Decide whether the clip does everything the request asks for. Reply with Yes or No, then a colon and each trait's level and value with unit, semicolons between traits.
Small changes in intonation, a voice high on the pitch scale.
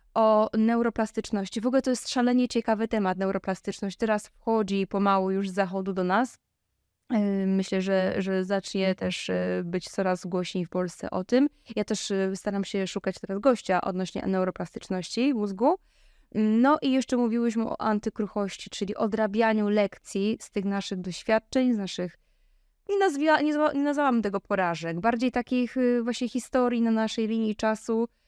No: average, 3.7 semitones; high, 215 Hz